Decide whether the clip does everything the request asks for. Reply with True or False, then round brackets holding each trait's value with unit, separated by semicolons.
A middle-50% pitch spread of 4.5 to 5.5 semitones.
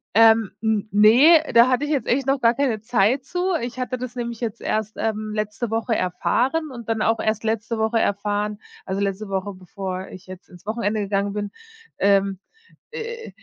False (3.3 semitones)